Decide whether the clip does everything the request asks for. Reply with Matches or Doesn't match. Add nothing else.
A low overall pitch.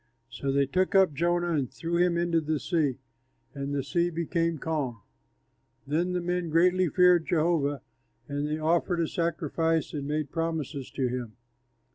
Doesn't match